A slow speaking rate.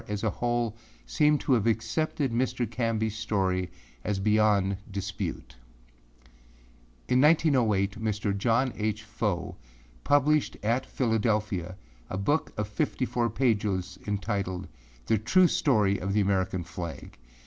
Yes: slow, 125 wpm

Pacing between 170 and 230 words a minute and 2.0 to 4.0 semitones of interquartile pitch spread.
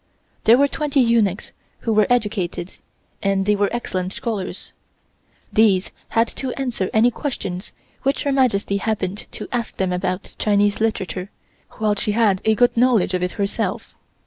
No: average, 155 wpm; average, 3.4 semitones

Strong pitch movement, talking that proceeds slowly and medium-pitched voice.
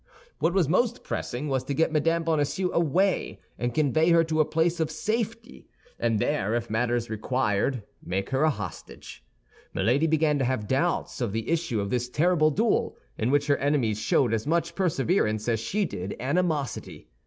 No: wide, 5.8 semitones; average, 175 wpm; medium, 145 Hz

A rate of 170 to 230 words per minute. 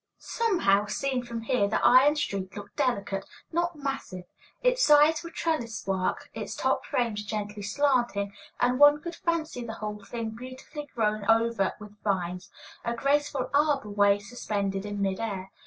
No: average, 155 wpm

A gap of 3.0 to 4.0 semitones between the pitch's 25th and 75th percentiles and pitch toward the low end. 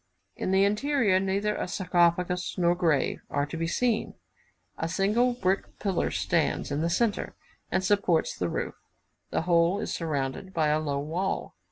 No: average, 3.4 semitones; medium, 180 Hz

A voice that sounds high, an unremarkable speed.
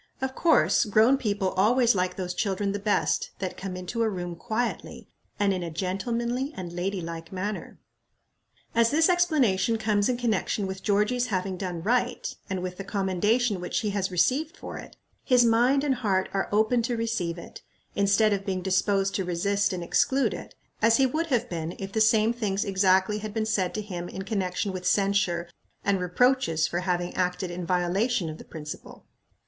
Yes: high, 200 Hz; average, 185 wpm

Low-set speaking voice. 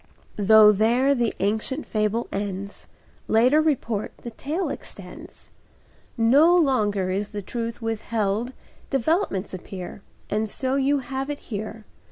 No: high, 225 Hz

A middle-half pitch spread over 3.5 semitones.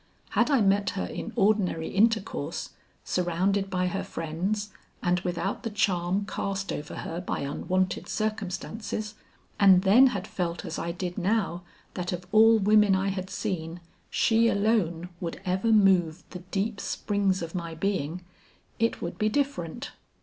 No: average, 3.0 semitones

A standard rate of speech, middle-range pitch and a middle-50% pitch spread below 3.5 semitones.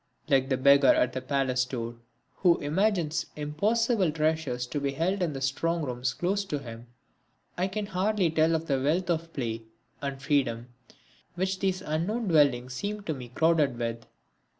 No: average, 170 wpm; medium, 150 Hz; wide, 5.4 semitones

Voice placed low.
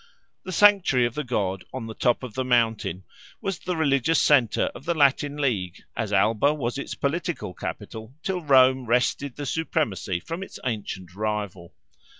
Yes: low, 125 Hz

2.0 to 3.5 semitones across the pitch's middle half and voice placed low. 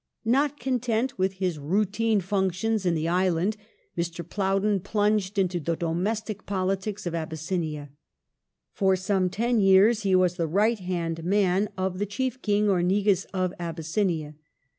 No: average, 3.1 semitones; high, 190 Hz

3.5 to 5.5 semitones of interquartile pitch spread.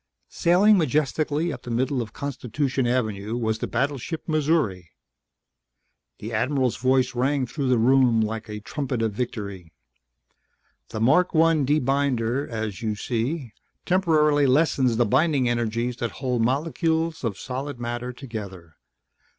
Yes: average, 4.2 semitones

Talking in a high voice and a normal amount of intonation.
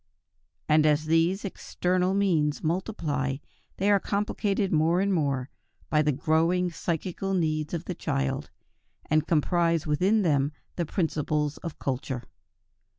No: medium, 160 Hz; average, 3.5 semitones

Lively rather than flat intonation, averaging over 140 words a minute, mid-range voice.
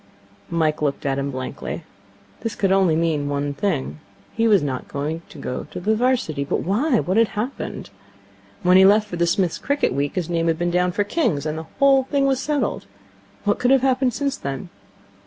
Yes: wide, 7.1 semitones; average, 200 wpm; medium, 180 Hz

